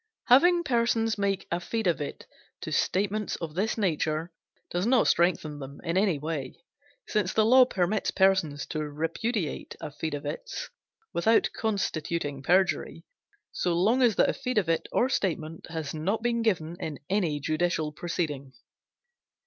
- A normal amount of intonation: No, wide, 5.7 semitones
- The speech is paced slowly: Yes, slow, 130 wpm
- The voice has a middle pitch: Yes, medium, 175 Hz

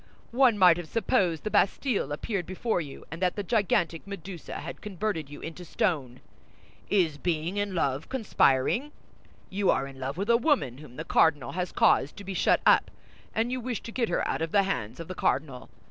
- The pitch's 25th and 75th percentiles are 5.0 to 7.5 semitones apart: Yes, average, 5.3 semitones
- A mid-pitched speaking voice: Yes, medium, 180 Hz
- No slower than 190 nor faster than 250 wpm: Yes, average, 200 wpm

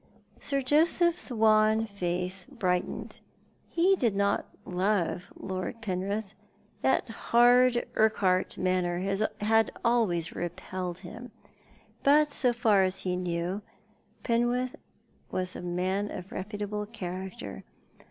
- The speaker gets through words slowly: Yes, slow, 105 wpm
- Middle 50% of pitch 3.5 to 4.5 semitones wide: Yes, average, 4.2 semitones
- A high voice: Yes, high, 200 Hz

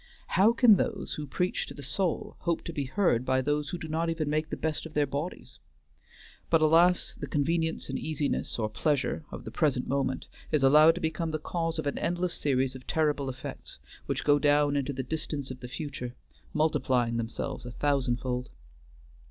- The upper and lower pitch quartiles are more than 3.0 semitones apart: Yes, average, 3.4 semitones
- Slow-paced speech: No, average, 195 wpm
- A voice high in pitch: No, medium, 150 Hz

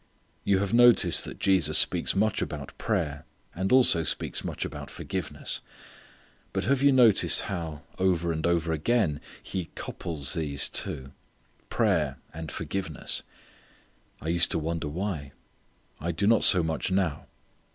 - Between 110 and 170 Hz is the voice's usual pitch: No, very low, 85 Hz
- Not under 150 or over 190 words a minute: No, average, 140 wpm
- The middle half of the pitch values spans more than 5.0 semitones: No, average, 3.8 semitones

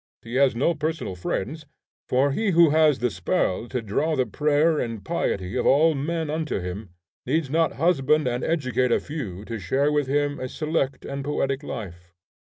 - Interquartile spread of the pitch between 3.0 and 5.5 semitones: Yes, average, 4.7 semitones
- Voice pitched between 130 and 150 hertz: Yes, medium, 140 Hz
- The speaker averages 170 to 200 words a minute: Yes, average, 180 wpm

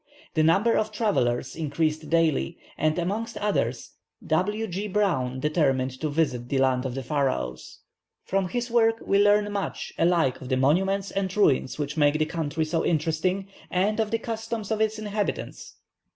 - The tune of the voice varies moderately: No, wide, 6.3 semitones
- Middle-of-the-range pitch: Yes, medium, 165 Hz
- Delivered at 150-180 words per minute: Yes, average, 165 wpm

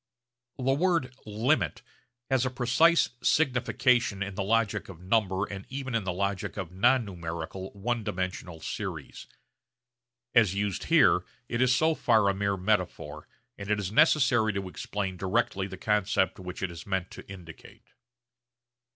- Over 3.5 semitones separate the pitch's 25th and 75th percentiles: Yes, average, 4.5 semitones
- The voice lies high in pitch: No, low, 100 Hz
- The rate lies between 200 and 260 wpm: No, average, 150 wpm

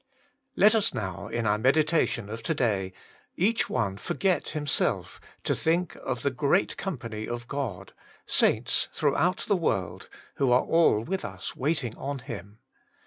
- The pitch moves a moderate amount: No, wide, 7.0 semitones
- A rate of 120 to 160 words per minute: Yes, average, 150 wpm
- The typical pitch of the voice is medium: No, low, 130 Hz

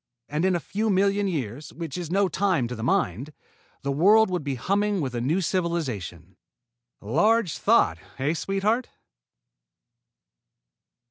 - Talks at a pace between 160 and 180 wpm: No, average, 140 wpm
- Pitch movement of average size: No, wide, 6.8 semitones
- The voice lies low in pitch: No, medium, 170 Hz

